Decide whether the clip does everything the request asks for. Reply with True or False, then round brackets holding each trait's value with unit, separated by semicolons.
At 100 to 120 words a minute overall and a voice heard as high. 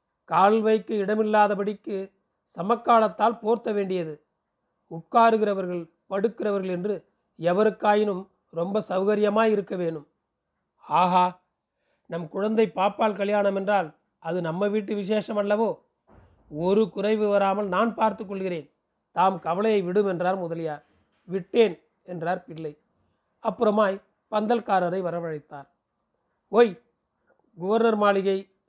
False (90 wpm; 200 Hz)